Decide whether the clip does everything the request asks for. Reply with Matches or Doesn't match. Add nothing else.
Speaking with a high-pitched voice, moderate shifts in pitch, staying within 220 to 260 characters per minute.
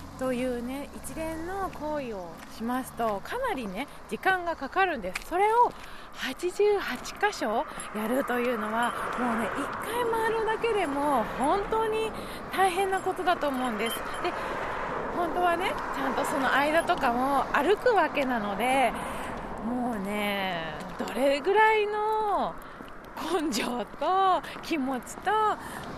Doesn't match